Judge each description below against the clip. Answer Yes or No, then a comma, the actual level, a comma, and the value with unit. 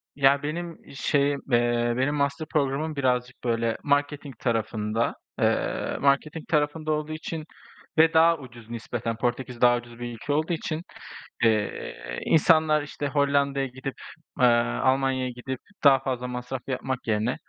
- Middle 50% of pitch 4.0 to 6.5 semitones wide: No, average, 3.4 semitones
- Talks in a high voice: No, low, 135 Hz